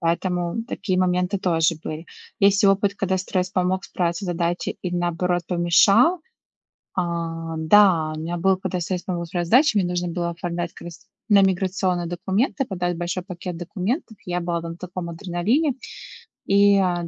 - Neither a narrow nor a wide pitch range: No, narrow, 2.0 semitones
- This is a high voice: No, medium, 180 Hz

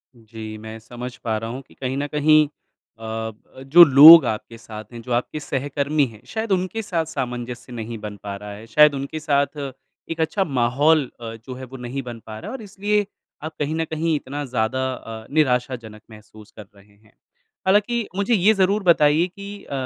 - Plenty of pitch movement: Yes, wide, 5.7 semitones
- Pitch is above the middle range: No, low, 135 Hz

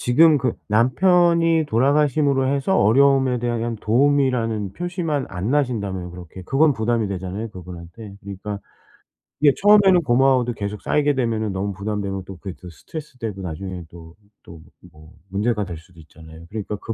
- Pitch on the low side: Yes, low, 115 Hz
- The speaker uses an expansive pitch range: Yes, wide, 6.4 semitones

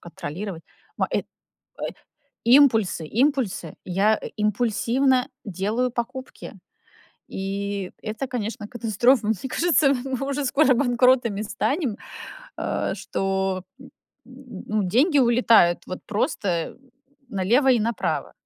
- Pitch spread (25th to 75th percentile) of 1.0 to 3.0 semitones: No, average, 4.6 semitones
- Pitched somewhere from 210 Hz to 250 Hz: Yes, high, 230 Hz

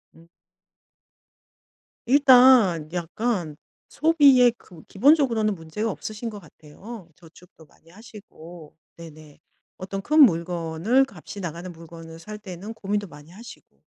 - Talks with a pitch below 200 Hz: Yes, high, 190 Hz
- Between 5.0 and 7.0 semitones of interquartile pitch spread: Yes, wide, 5.6 semitones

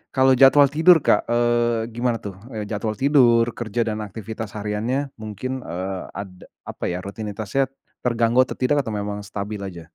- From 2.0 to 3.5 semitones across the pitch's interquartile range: Yes, average, 3.0 semitones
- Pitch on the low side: Yes, low, 110 Hz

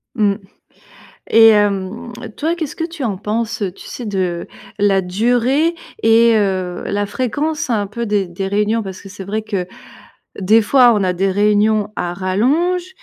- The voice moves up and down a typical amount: Yes, average, 3.5 semitones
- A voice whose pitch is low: No, high, 210 Hz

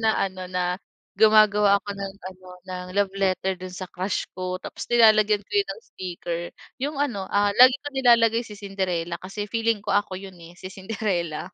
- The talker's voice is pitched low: No, high, 195 Hz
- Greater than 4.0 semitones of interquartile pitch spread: No, average, 2.9 semitones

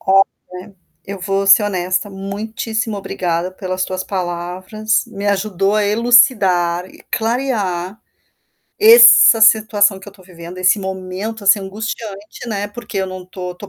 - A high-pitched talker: Yes, high, 195 Hz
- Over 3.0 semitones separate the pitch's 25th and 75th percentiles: No, average, 2.7 semitones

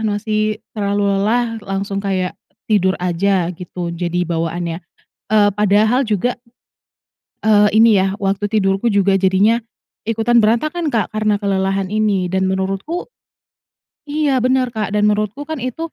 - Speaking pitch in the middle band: No, high, 205 Hz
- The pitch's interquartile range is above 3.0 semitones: No, average, 2.7 semitones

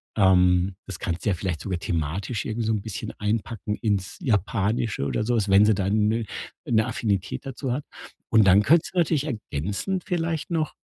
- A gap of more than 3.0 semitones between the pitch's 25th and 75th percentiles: Yes, average, 3.7 semitones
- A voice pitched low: Yes, low, 105 Hz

